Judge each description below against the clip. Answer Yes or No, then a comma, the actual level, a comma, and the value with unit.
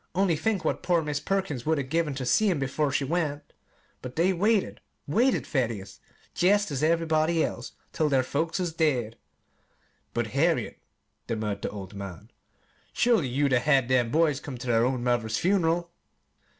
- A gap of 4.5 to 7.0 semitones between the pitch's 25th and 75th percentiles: Yes, average, 5.1 semitones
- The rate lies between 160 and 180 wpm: Yes, average, 170 wpm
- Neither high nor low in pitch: Yes, medium, 150 Hz